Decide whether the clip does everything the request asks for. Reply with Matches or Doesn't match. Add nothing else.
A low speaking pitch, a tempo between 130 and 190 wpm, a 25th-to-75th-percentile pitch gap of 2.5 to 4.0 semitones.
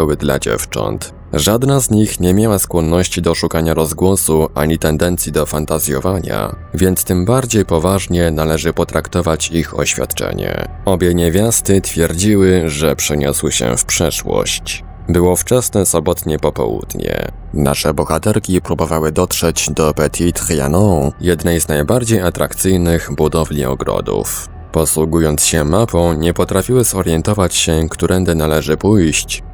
Doesn't match